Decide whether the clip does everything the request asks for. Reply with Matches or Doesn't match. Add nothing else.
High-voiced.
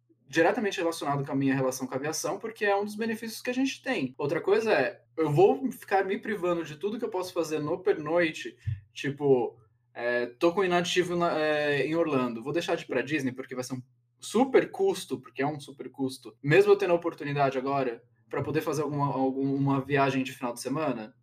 Doesn't match